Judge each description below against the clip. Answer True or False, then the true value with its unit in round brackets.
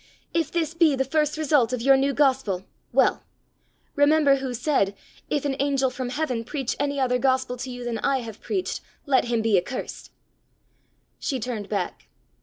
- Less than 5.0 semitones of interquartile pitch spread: True (2.9 semitones)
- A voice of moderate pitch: False (265 Hz)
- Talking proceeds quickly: False (175 wpm)